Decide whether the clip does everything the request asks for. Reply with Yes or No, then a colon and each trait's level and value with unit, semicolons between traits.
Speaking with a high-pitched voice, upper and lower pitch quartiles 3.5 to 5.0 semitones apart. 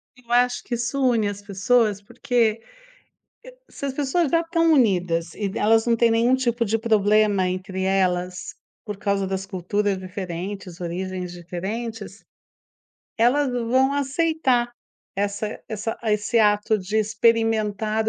Yes: high, 215 Hz; average, 3.8 semitones